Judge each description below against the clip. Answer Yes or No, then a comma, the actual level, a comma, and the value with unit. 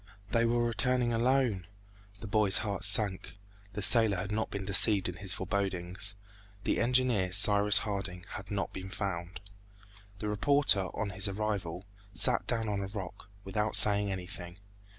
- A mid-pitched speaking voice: No, low, 100 Hz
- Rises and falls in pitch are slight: Yes, narrow, 2.3 semitones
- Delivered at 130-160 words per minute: Yes, average, 150 wpm